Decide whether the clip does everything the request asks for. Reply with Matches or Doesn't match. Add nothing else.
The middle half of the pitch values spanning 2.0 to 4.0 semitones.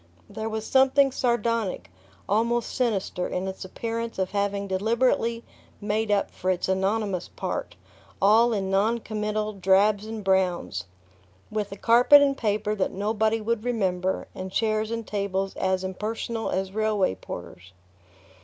Matches